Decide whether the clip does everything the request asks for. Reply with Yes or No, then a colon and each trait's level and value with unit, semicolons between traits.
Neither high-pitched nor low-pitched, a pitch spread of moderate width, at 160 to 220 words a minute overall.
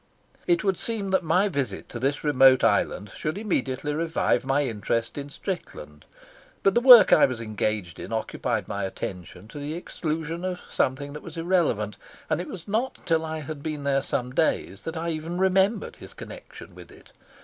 No: medium, 155 Hz; wide, 5.9 semitones; average, 185 wpm